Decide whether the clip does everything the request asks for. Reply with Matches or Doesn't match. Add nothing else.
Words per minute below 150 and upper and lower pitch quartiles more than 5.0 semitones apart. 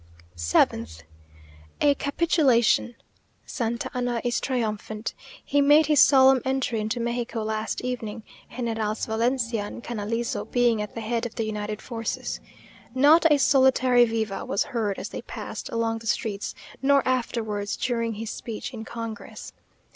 Doesn't match